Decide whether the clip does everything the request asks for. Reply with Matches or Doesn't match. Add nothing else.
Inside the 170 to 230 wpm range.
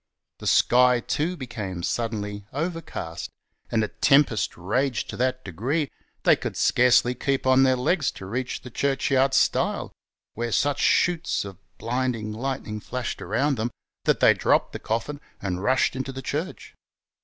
Doesn't match